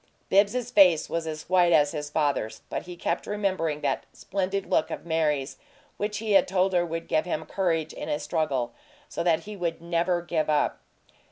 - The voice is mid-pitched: Yes, medium, 170 Hz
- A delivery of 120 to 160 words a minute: No, average, 190 wpm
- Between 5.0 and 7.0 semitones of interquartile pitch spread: No, average, 3.3 semitones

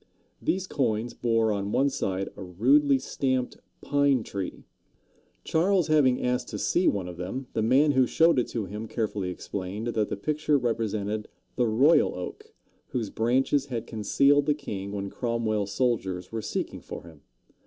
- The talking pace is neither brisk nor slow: Yes, average, 165 wpm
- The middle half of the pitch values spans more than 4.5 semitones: Yes, average, 5.2 semitones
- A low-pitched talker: Yes, low, 115 Hz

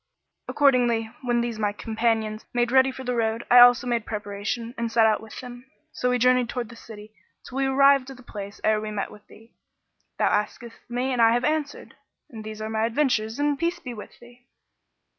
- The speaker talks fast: Yes, fast, 210 wpm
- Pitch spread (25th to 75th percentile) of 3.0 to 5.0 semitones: No, narrow, 2.4 semitones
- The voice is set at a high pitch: Yes, high, 235 Hz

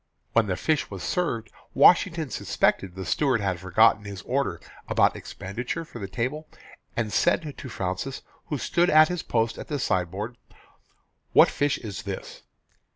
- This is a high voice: No, low, 115 Hz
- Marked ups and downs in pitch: Yes, wide, 6.9 semitones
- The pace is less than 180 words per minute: Yes, average, 155 wpm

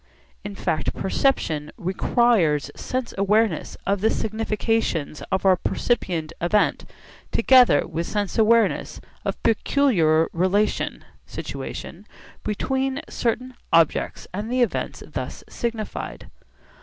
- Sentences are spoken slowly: Yes, slow, 105 wpm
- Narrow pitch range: No, average, 5.2 semitones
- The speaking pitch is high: Yes, high, 210 Hz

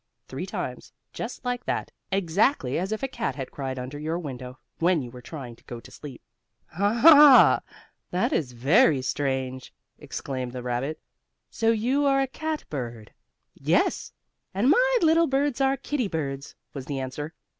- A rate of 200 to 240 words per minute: No, average, 165 wpm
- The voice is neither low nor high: Yes, medium, 155 Hz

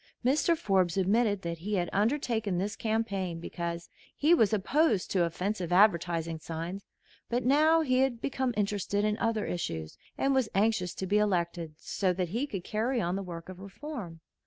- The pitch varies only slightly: No, average, 4.8 semitones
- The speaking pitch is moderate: No, high, 200 Hz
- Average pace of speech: Yes, average, 175 wpm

